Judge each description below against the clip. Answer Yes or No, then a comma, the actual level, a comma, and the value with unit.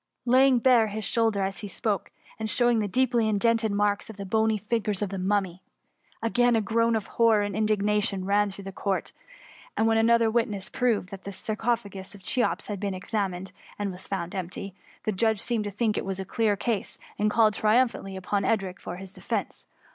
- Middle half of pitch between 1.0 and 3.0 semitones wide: Yes, narrow, 2.6 semitones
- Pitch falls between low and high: No, high, 210 Hz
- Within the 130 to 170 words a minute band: No, fast, 205 wpm